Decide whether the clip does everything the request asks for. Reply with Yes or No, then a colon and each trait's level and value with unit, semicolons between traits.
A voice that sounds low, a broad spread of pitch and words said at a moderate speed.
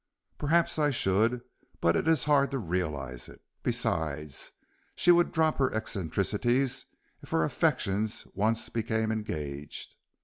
No: low, 110 Hz; wide, 8.7 semitones; slow, 130 wpm